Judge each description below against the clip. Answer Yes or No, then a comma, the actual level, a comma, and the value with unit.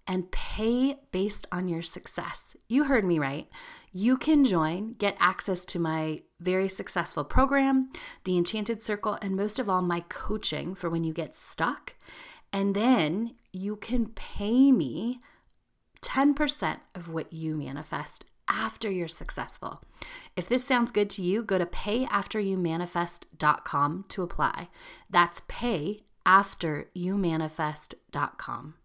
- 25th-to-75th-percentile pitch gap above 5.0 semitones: Yes, wide, 5.4 semitones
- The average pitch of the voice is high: Yes, high, 195 Hz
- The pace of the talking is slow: Yes, slow, 125 wpm